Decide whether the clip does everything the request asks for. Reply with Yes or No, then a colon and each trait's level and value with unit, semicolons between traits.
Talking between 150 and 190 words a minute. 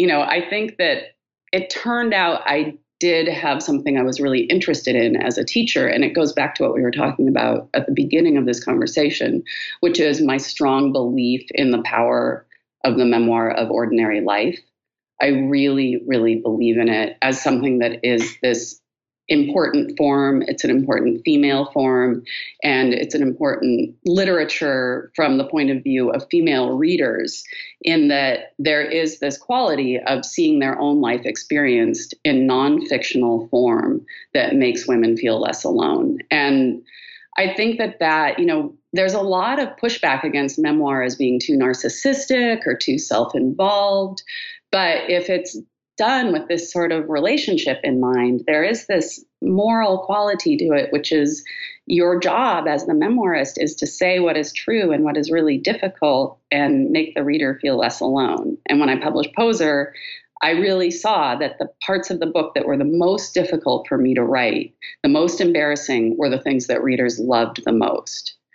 Yes: average, 175 wpm